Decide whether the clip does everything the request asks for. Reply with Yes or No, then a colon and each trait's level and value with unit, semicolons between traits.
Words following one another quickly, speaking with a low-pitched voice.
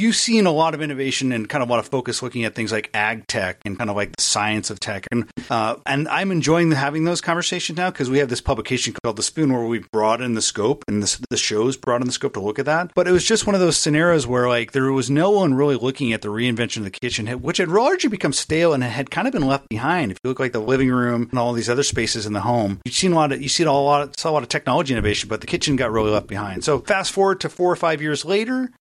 Yes: fast, 300 wpm; low, 130 Hz